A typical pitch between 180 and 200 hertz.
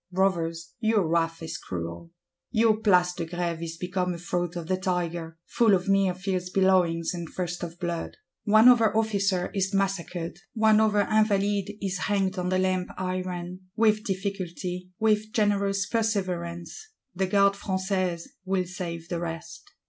Yes: medium, 185 Hz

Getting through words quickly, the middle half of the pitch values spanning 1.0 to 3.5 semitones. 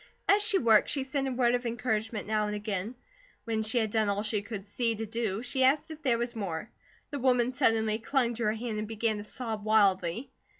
Yes: fast, 225 wpm; narrow, 2.6 semitones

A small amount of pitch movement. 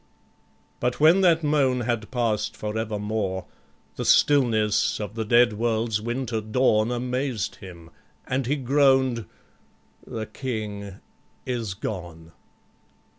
No: average, 3.3 semitones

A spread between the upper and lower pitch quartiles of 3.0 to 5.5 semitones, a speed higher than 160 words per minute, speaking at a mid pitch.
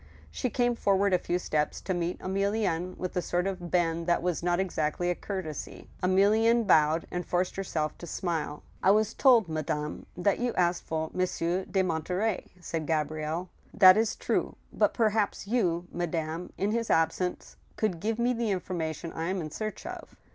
Yes: average, 3.4 semitones; average, 185 wpm; medium, 180 Hz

